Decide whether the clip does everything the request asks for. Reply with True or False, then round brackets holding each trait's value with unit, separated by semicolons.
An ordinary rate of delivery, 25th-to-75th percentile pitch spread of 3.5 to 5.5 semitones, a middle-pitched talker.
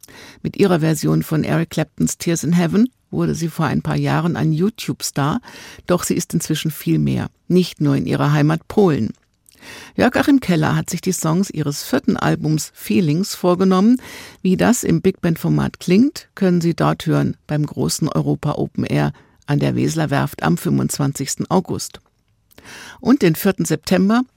True (165 wpm; 4.2 semitones; 170 Hz)